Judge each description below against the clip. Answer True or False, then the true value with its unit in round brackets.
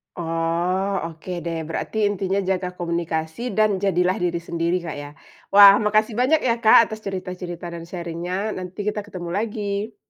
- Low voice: False (185 Hz)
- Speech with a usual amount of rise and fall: True (3.2 semitones)